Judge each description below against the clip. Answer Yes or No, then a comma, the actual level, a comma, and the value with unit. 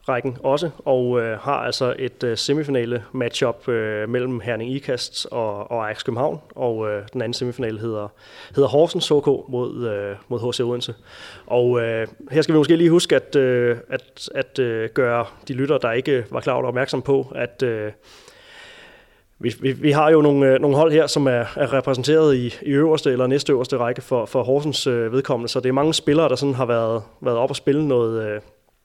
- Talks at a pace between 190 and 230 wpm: Yes, average, 205 wpm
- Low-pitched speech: Yes, low, 125 Hz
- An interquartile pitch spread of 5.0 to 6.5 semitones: No, average, 3.4 semitones